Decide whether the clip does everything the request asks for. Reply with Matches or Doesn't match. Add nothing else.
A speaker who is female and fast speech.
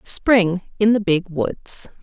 Doesn't match